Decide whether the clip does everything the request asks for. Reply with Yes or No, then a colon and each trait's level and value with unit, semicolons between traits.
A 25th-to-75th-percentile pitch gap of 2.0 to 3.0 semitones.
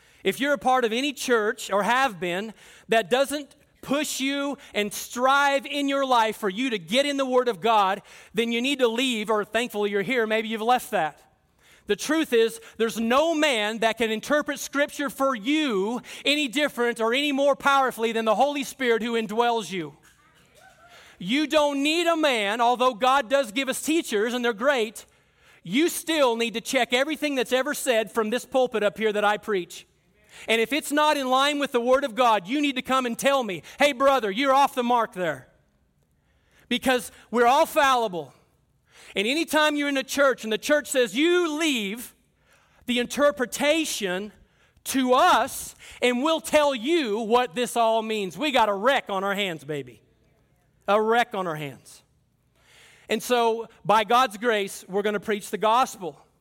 No: average, 4.4 semitones